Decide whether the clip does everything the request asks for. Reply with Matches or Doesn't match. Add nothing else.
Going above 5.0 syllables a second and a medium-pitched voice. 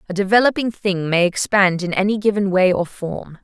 Doesn't match